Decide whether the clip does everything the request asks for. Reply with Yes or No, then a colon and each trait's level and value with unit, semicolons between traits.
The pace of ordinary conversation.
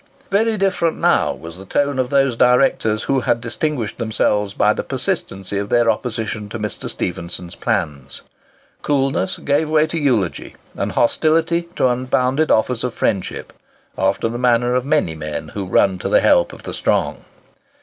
Yes: average, 160 wpm